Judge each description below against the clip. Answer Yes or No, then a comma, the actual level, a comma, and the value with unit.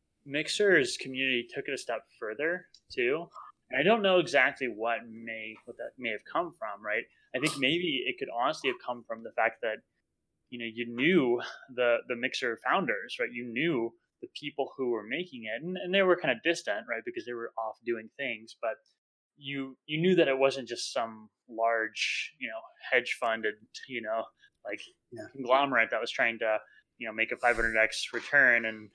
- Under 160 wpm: No, average, 195 wpm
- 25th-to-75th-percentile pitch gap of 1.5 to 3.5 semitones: No, average, 3.9 semitones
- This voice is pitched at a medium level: No, low, 120 Hz